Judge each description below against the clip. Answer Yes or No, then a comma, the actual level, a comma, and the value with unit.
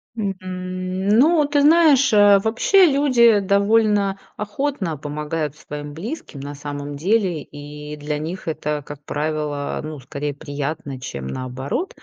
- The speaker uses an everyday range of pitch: No, wide, 6.6 semitones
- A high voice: No, medium, 170 Hz